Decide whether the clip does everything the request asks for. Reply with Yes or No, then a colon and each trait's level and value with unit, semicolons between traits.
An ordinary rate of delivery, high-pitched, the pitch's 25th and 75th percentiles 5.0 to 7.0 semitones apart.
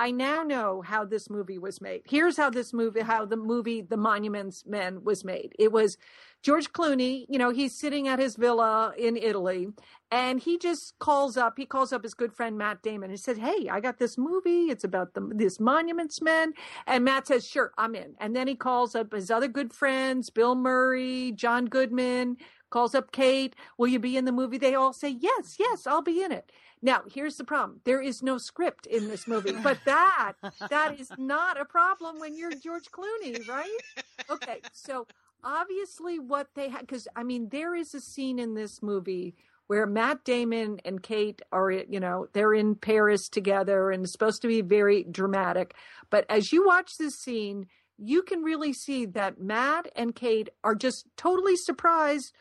Yes: average, 195 wpm; very high, 255 Hz; average, 5.3 semitones